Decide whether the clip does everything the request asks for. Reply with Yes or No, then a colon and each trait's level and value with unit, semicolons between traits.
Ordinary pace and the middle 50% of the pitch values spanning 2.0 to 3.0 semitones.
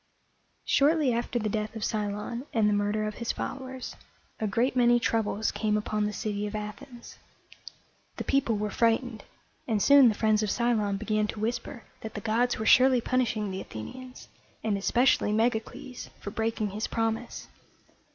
Yes: average, 165 wpm; narrow, 2.5 semitones